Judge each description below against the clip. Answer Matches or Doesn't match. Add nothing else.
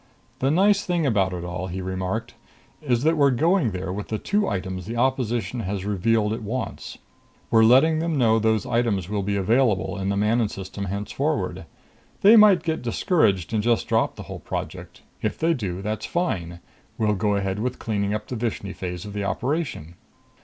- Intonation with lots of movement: Doesn't match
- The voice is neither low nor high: Doesn't match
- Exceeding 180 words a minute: Matches